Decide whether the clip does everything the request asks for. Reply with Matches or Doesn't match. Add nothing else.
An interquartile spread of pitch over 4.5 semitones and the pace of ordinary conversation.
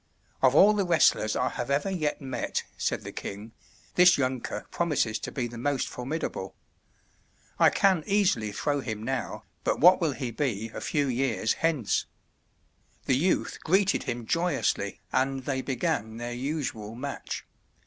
Matches